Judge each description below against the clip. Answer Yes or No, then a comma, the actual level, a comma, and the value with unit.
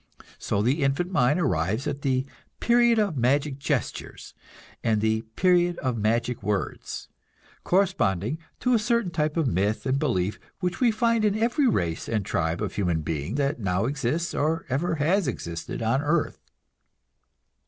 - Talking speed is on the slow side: No, average, 155 wpm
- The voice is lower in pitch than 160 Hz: Yes, medium, 140 Hz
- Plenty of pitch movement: Yes, wide, 8.3 semitones